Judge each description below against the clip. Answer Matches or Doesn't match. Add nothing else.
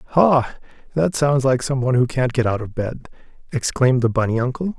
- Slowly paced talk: Doesn't match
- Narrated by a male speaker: Matches